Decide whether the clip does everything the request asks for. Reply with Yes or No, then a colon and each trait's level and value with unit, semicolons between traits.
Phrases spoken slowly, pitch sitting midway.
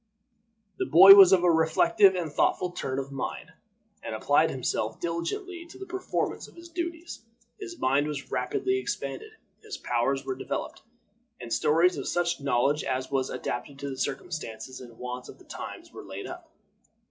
No: average, 170 wpm; medium, 160 Hz